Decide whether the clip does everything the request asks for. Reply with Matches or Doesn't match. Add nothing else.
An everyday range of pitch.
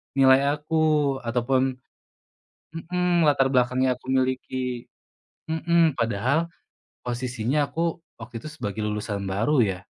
Matches